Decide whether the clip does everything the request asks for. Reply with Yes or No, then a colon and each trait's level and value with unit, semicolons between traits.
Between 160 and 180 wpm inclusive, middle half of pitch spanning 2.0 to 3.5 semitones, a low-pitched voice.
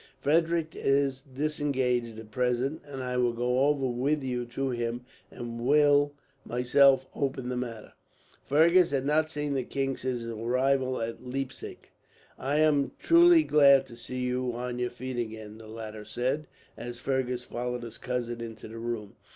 Yes: average, 165 wpm; average, 2.7 semitones; low, 125 Hz